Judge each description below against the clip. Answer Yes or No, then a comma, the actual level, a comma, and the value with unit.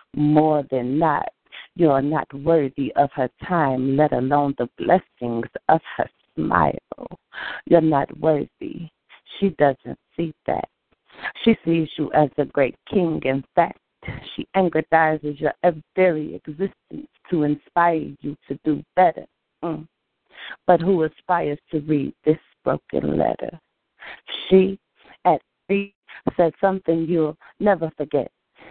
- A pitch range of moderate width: Yes, average, 3.2 semitones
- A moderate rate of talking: No, slow, 125 wpm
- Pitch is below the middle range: No, medium, 155 Hz